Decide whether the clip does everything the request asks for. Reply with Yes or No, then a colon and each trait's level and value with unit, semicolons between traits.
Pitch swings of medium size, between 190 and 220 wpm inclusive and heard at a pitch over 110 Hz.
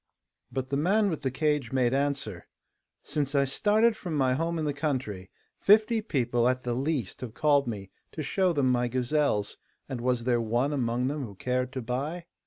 Yes: average, 3.8 semitones; average, 195 wpm; low, 135 Hz